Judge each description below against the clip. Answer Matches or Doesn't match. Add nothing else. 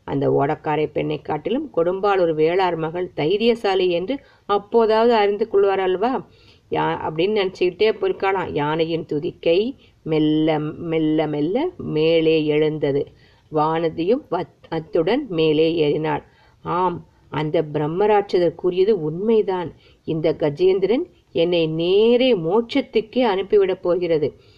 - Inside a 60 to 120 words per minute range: Matches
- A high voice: Doesn't match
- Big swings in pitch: Matches